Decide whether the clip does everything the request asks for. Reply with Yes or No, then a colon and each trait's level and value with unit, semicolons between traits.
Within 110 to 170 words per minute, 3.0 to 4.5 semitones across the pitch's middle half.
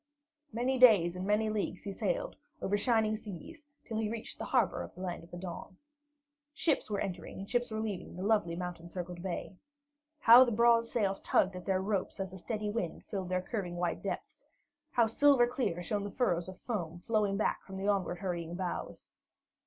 No: average, 200 wpm; average, 3.9 semitones